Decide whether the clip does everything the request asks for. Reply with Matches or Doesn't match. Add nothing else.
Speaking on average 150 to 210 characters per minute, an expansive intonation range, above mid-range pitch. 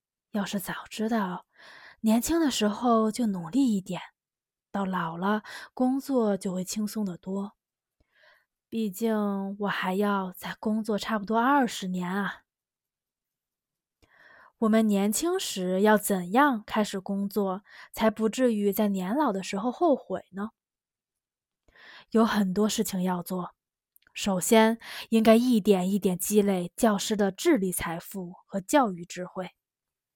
Doesn't match